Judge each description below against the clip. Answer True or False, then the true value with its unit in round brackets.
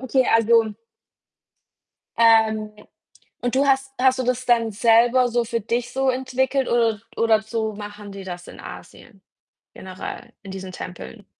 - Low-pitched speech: False (230 Hz)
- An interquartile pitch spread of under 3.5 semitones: True (3.1 semitones)